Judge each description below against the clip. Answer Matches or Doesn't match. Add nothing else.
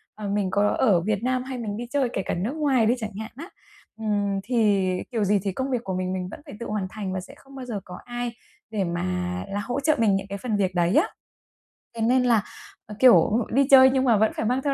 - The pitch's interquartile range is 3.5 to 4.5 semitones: Matches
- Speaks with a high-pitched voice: Matches